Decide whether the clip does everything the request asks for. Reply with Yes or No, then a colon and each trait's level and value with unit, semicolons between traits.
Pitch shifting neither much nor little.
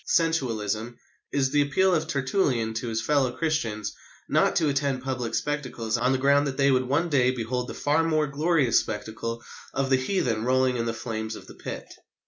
Yes: average, 3.9 semitones